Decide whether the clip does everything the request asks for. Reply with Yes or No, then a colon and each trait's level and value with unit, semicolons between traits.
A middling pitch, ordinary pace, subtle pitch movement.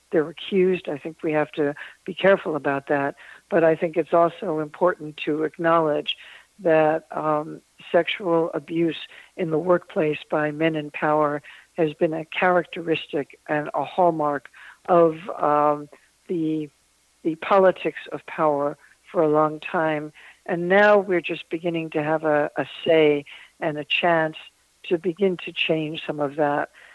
Yes: medium, 160 Hz; average, 150 wpm; narrow, 2.3 semitones